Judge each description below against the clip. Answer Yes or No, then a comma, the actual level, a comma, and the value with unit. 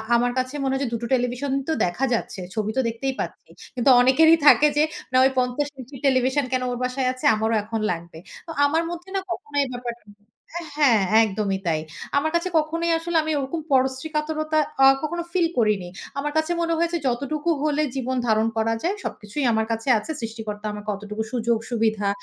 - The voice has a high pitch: Yes, very high, 255 Hz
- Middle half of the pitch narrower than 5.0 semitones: No, average, 5.3 semitones